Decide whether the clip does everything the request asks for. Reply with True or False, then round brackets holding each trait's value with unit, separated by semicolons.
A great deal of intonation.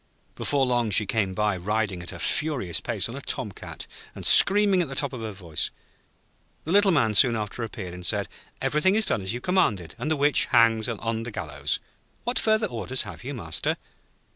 True (6.4 semitones)